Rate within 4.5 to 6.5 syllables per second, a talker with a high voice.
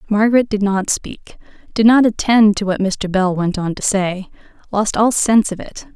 Yes: 4.9 syllables/s; high, 205 Hz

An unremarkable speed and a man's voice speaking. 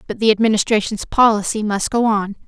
No: average, 170 wpm; female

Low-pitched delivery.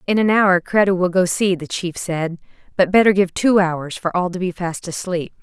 No: medium, 180 Hz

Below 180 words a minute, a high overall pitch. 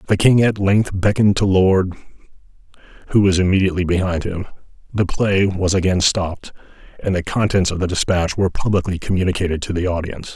No: average, 170 wpm; very low, 95 Hz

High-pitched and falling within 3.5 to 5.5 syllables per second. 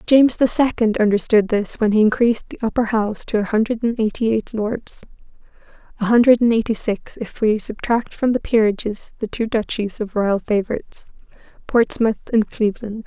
Yes: high, 220 Hz; 5.4 syllables/s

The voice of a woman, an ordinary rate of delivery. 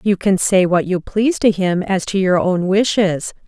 No: female; fast, 225 wpm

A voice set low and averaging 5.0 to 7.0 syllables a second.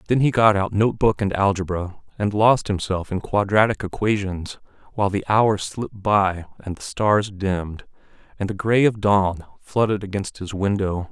No: low, 100 Hz; 4.7 syllables/s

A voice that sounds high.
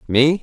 No: medium, 145 Hz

